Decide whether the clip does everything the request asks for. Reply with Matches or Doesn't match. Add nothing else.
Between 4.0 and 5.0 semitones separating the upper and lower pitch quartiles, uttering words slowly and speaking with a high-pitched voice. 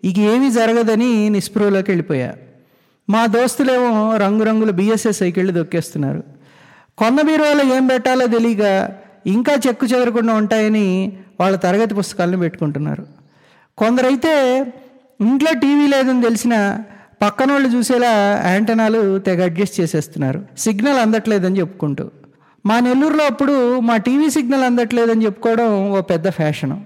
Matches